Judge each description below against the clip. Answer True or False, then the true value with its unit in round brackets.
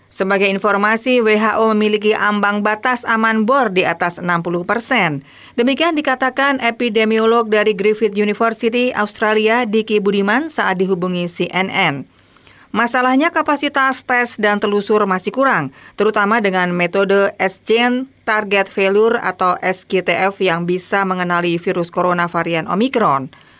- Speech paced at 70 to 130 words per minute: True (115 wpm)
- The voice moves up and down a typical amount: True (4.0 semitones)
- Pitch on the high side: True (210 Hz)